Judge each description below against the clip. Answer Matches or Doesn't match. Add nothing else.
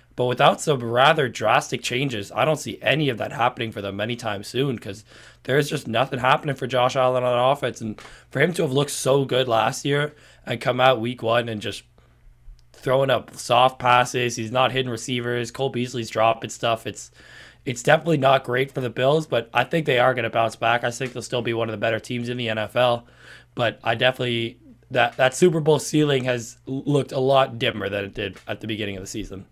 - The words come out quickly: Matches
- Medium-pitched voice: Doesn't match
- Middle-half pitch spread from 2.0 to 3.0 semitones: Matches